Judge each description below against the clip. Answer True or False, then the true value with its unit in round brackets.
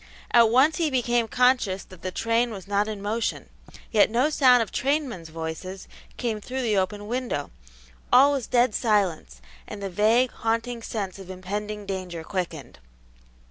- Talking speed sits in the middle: True (160 wpm)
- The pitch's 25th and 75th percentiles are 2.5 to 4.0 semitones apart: False (4.5 semitones)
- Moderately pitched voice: False (215 Hz)